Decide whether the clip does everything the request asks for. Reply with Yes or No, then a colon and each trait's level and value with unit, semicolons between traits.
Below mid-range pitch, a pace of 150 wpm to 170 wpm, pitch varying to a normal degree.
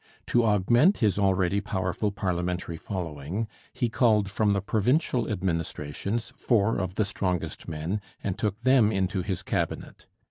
No: low, 100 Hz; average, 140 wpm; average, 3.3 semitones